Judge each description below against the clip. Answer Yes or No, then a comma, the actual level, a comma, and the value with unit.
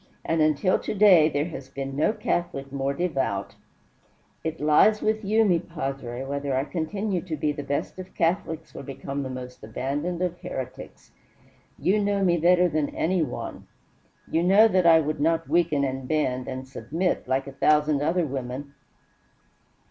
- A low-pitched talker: No, medium, 155 Hz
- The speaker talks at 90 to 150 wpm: No, average, 170 wpm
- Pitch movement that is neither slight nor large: Yes, average, 4.5 semitones